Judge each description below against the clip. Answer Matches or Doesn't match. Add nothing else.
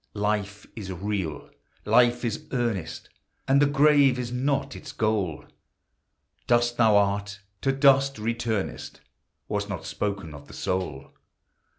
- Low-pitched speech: Matches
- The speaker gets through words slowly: Matches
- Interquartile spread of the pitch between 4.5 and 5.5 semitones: Doesn't match